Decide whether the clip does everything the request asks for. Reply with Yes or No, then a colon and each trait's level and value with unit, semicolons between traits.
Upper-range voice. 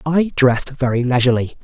No: low, 135 Hz